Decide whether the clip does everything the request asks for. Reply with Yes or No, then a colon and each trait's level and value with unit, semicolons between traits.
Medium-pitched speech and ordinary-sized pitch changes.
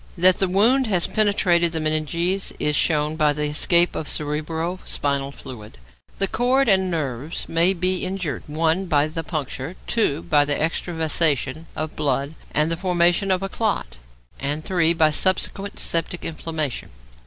Yes: medium, 165 Hz; average, 3.6 semitones